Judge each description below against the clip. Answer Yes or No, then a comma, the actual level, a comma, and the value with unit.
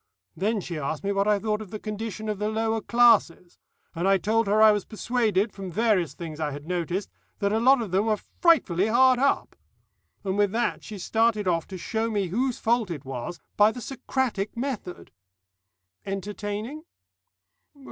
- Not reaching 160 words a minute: No, average, 175 wpm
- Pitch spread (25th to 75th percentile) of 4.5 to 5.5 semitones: No, average, 3.2 semitones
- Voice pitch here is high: Yes, high, 210 Hz